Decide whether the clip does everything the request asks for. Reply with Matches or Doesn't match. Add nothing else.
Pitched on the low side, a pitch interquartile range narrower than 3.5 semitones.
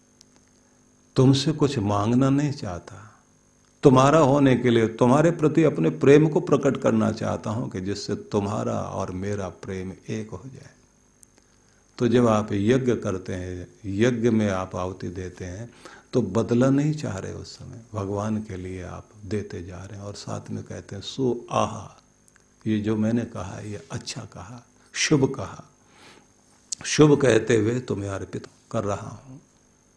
Doesn't match